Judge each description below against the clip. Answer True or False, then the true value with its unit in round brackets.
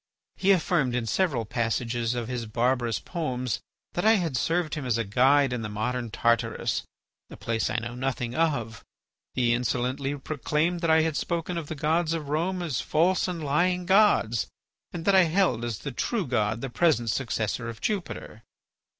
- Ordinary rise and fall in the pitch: False (6.1 semitones)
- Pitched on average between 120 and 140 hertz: True (135 Hz)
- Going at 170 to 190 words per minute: True (180 wpm)